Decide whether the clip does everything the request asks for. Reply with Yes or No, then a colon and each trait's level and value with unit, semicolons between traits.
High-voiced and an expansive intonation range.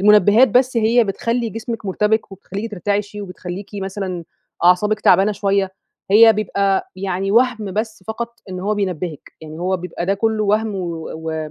No: high, 200 Hz; average, 2.8 semitones